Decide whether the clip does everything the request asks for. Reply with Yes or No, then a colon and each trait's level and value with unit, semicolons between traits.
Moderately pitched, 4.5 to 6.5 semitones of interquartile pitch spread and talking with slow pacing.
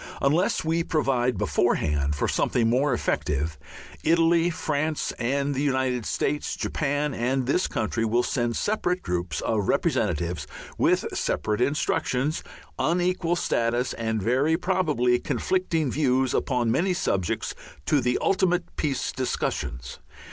No: low, 130 Hz; wide, 5.6 semitones; slow, 120 wpm